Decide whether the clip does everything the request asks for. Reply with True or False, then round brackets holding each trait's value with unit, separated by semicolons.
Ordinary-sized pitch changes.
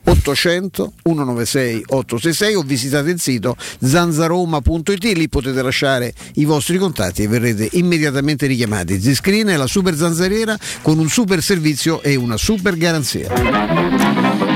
False (5.9 semitones)